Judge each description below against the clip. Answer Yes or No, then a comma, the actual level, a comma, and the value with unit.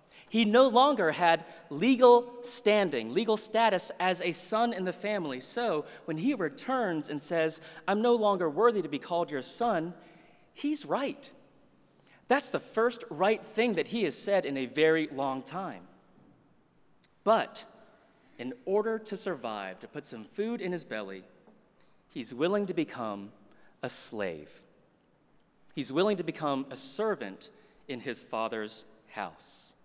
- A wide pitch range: Yes, wide, 7.2 semitones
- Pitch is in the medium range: Yes, medium, 180 Hz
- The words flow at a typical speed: Yes, average, 145 wpm